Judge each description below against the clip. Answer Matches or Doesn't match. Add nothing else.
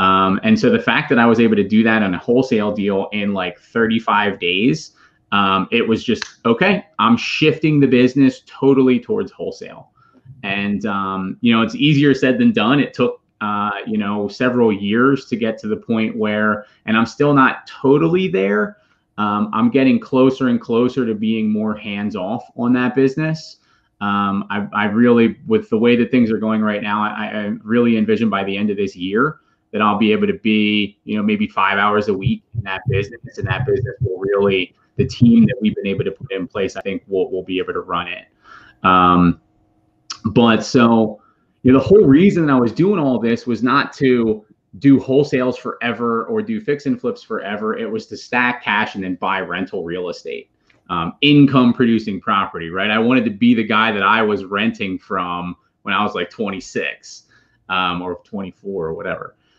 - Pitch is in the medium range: Doesn't match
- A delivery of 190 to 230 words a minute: Matches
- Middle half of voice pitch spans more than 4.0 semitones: Matches